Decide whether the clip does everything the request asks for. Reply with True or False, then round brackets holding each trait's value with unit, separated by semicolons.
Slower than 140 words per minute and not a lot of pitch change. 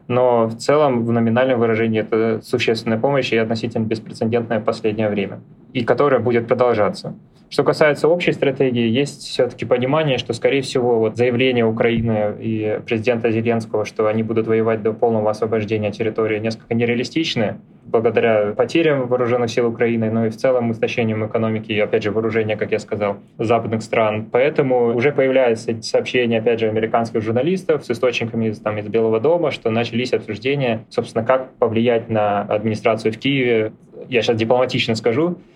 False (155 wpm; 2.0 semitones)